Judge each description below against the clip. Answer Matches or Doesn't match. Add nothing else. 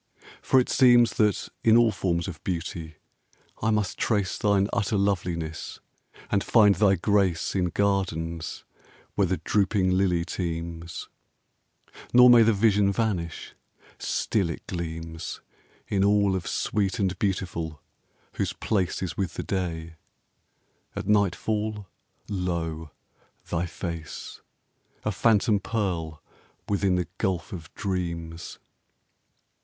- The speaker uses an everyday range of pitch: Matches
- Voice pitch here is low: Matches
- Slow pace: Matches